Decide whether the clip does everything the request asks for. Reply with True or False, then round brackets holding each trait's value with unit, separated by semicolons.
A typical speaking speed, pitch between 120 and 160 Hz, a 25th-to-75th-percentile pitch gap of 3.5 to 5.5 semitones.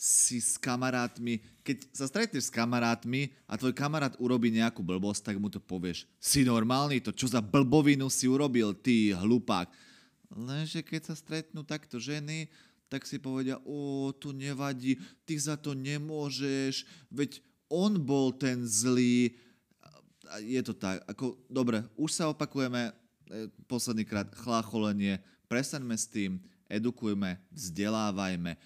True (140 wpm; 125 Hz; 3.9 semitones)